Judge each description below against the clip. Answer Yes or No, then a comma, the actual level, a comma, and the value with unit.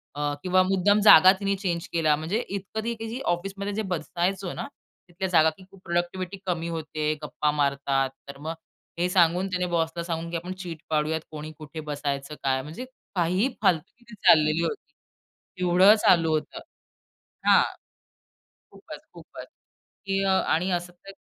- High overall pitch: No, medium, 175 Hz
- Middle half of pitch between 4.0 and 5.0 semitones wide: No, average, 3.5 semitones